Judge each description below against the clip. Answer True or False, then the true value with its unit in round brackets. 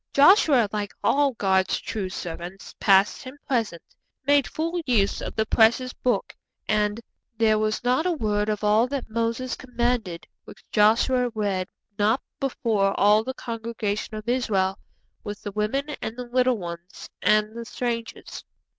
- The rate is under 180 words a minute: True (150 wpm)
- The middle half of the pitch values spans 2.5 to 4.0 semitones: True (3.3 semitones)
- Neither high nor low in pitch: False (220 Hz)